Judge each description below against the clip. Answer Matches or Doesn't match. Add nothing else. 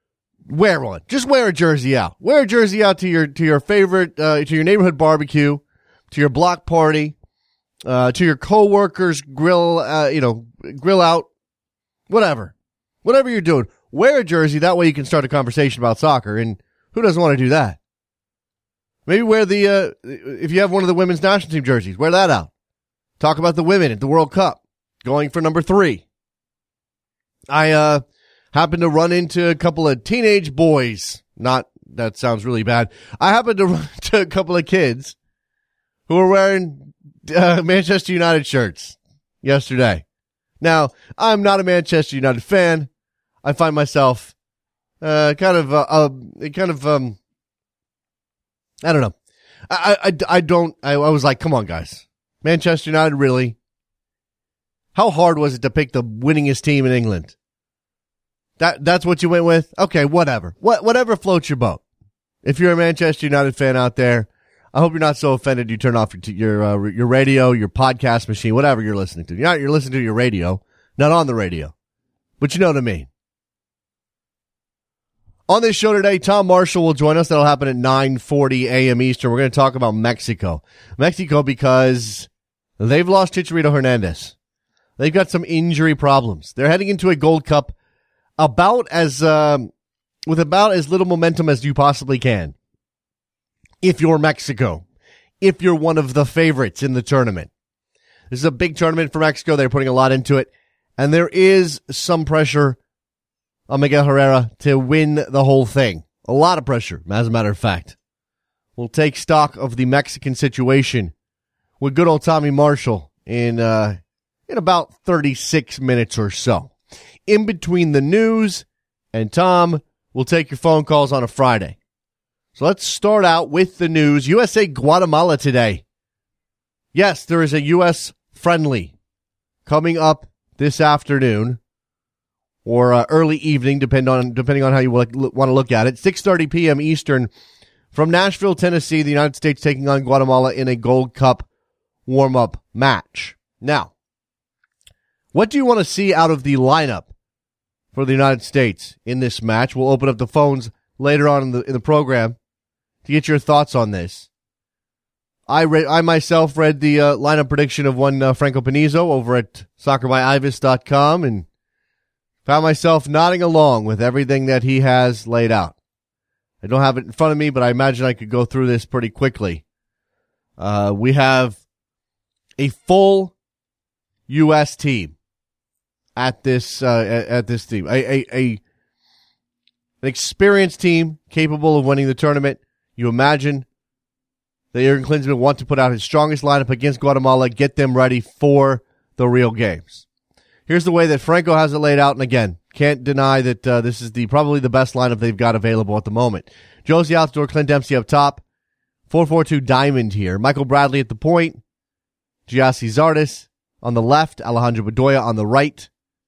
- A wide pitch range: Doesn't match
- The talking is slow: Doesn't match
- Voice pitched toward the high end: Doesn't match